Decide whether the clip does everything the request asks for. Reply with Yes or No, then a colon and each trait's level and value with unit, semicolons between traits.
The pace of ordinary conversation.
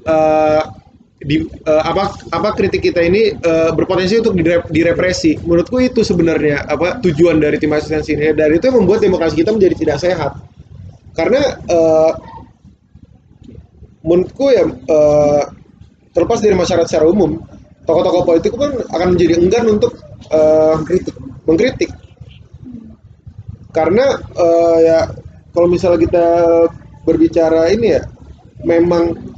Yes: average, 125 wpm